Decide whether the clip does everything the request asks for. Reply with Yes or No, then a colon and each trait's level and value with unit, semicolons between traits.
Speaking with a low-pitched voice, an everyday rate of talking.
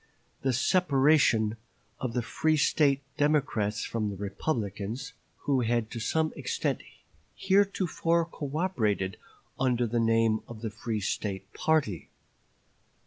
No: low, 120 Hz; slow, 115 wpm